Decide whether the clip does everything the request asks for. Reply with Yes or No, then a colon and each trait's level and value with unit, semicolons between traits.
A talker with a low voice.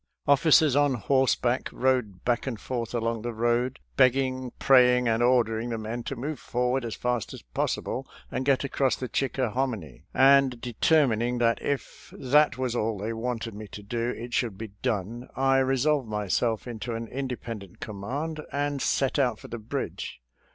Yes: low, 125 Hz